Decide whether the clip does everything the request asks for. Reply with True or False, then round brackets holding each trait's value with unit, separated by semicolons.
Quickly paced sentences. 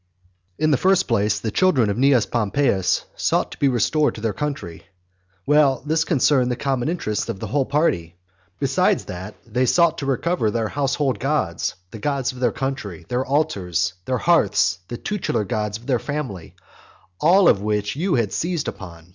False (180 wpm)